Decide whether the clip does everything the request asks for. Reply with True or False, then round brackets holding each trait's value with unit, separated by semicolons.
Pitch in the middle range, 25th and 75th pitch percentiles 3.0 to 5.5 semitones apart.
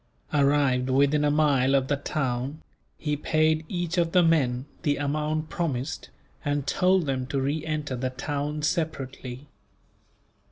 False (145 Hz; 2.6 semitones)